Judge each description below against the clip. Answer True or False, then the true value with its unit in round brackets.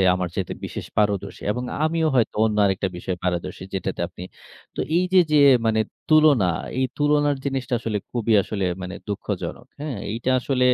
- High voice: False (115 Hz)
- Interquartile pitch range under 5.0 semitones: False (7.2 semitones)